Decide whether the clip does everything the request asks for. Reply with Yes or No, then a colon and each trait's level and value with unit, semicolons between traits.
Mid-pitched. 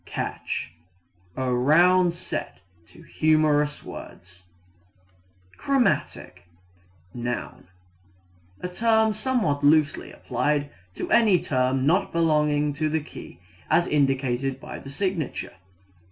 Yes: medium, 150 Hz